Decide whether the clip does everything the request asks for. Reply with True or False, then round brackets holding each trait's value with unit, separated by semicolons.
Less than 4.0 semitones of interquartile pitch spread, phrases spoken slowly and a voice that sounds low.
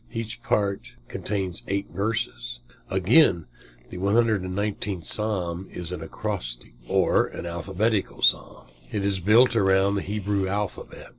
True (2.4 semitones; 125 wpm; 100 Hz)